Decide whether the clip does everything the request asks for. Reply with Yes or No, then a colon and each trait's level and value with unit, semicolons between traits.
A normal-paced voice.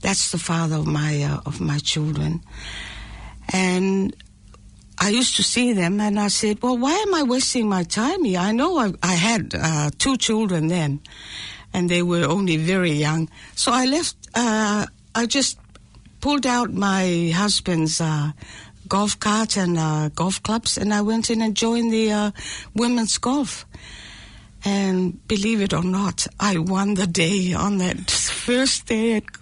Yes: average, 170 wpm